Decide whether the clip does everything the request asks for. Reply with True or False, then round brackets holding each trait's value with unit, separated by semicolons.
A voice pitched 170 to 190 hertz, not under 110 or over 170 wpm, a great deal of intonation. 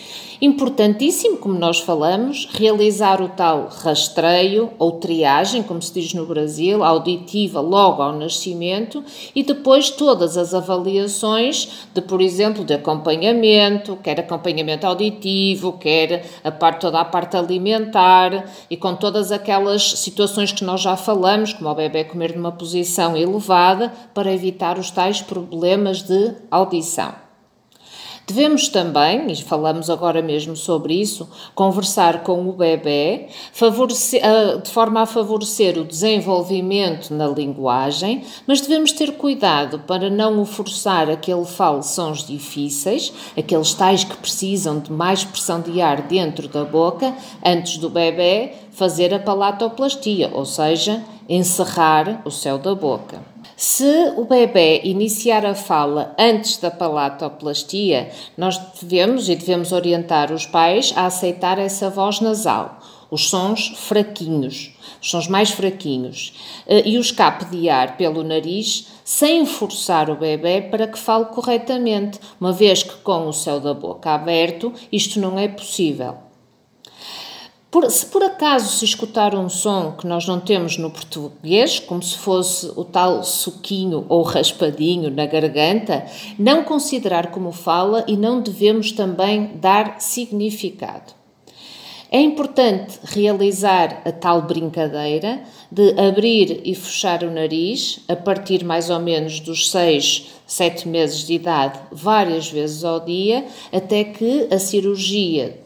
False (185 Hz; 135 wpm; 4.0 semitones)